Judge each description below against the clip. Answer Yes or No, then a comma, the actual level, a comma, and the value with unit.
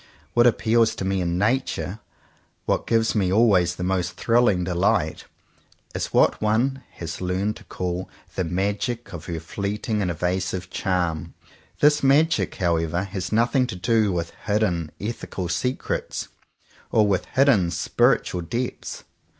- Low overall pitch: Yes, very low, 95 Hz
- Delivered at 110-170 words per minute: Yes, average, 140 wpm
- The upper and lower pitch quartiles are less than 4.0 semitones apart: No, average, 4.4 semitones